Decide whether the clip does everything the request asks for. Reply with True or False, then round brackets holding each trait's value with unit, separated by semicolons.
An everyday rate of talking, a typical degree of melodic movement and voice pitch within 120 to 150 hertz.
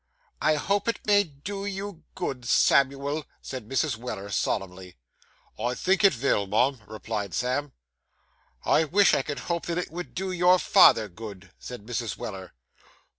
False (155 wpm; 8.4 semitones; 140 Hz)